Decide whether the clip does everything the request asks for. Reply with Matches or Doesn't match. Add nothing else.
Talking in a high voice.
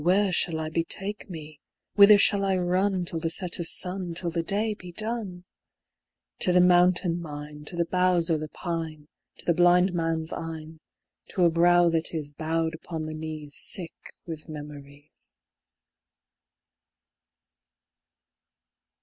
Doesn't match